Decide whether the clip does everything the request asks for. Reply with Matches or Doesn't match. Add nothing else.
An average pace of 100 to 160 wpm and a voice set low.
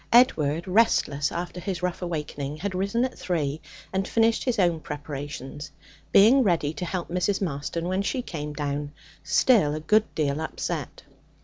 Doesn't match